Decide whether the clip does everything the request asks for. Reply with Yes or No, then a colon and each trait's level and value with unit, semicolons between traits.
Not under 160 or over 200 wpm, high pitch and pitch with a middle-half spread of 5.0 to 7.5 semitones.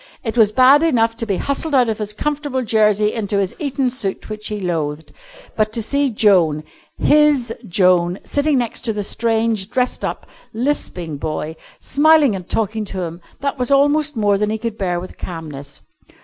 Yes: average, 175 wpm; high, 220 Hz; wide, 5.4 semitones